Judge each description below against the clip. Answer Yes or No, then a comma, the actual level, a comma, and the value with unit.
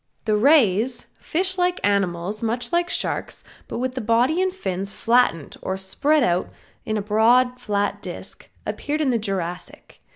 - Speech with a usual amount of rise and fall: No, wide, 6.0 semitones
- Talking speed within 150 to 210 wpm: Yes, average, 160 wpm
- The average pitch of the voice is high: Yes, high, 230 Hz